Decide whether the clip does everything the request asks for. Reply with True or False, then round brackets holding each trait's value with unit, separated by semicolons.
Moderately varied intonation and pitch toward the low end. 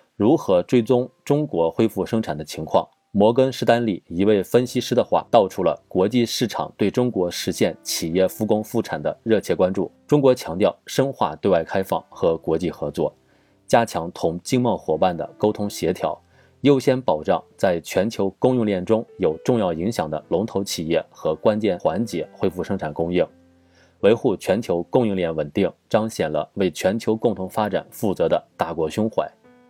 True (4.9 semitones; 110 Hz)